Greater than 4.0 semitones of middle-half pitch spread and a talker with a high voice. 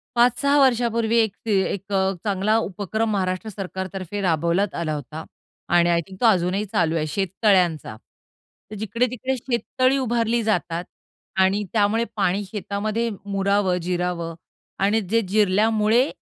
No: average, 3.5 semitones; high, 200 Hz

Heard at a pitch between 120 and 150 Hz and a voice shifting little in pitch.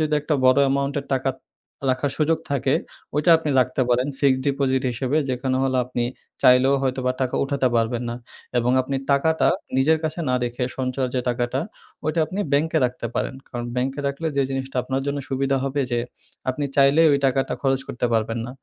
Yes: low, 135 Hz; narrow, 1.8 semitones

